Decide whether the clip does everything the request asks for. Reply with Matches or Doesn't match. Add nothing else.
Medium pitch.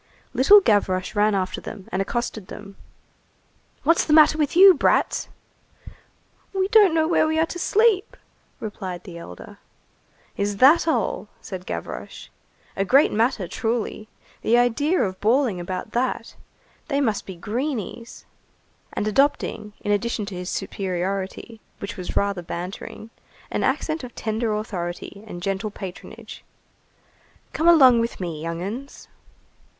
Doesn't match